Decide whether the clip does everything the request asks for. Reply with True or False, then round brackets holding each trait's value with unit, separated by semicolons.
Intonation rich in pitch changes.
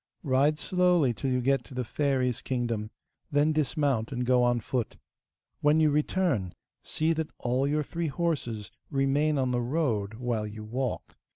False (3.8 semitones)